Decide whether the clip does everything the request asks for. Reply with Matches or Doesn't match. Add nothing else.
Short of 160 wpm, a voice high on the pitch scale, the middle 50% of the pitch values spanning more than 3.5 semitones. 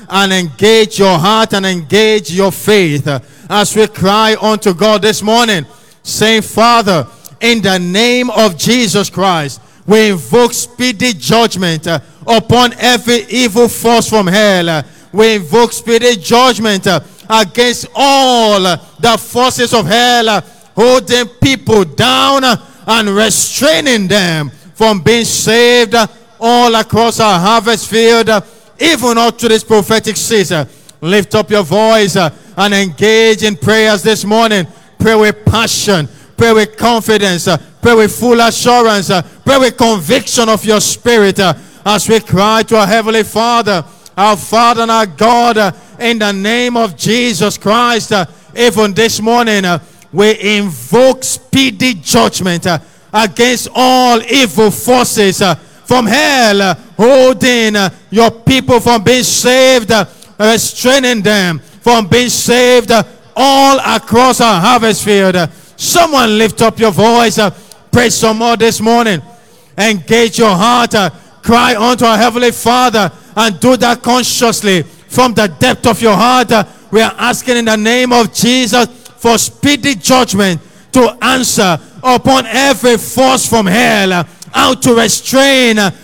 Doesn't match